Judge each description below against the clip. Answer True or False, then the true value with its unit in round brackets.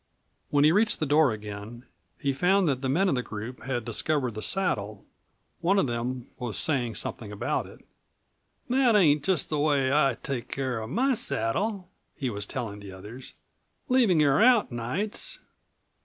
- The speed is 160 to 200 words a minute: True (170 wpm)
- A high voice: False (135 Hz)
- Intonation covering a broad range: True (7.4 semitones)